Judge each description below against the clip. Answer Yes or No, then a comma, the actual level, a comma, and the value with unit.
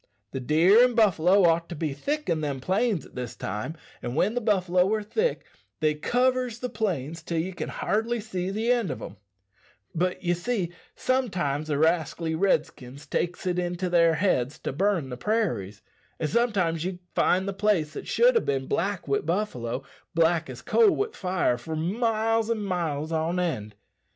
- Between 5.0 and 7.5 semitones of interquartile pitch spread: Yes, wide, 5.4 semitones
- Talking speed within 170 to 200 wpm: Yes, average, 185 wpm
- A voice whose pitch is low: No, medium, 175 Hz